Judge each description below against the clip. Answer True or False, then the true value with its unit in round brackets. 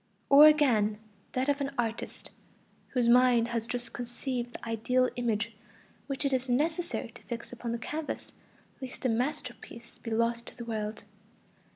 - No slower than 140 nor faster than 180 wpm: True (160 wpm)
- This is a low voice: False (245 Hz)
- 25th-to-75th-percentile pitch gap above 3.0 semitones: False (2.4 semitones)